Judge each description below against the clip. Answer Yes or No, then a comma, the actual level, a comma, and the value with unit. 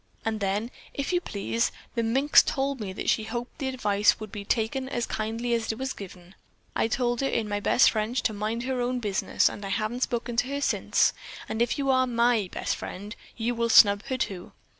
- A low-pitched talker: No, high, 230 Hz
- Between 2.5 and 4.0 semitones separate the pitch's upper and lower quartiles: Yes, average, 3.1 semitones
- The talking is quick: Yes, fast, 215 wpm